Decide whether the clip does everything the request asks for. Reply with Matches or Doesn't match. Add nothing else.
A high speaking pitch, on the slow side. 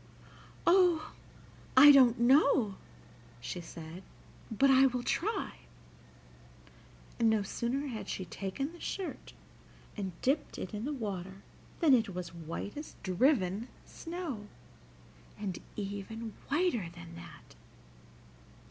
Matches